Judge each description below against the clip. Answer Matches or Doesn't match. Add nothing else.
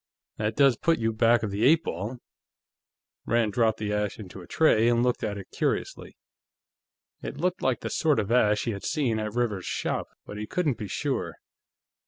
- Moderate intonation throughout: Matches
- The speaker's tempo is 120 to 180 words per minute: Doesn't match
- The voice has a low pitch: Matches